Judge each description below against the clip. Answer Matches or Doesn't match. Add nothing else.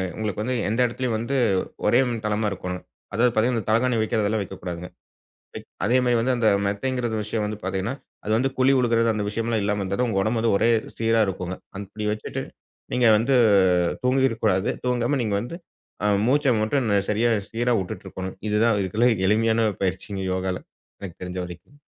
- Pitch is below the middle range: Matches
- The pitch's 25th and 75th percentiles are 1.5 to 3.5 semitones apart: Matches